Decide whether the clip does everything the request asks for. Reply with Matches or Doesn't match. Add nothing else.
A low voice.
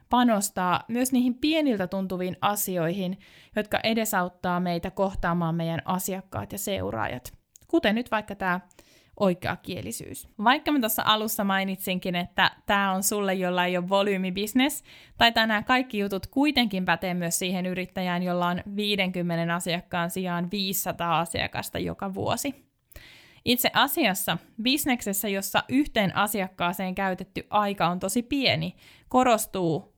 Doesn't match